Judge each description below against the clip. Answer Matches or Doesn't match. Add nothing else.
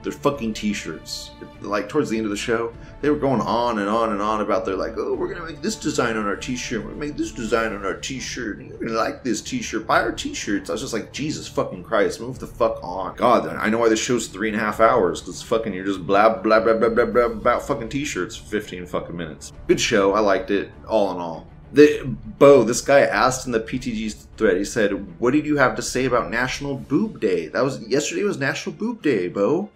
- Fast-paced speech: Matches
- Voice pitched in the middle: Doesn't match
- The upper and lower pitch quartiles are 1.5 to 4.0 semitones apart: Doesn't match